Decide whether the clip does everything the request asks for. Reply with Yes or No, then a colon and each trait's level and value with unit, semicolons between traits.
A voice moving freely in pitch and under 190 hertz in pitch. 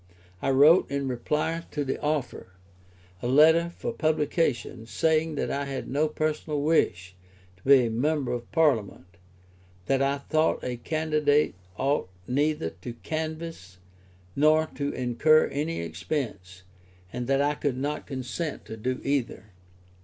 No: average, 4.0 semitones; medium, 140 Hz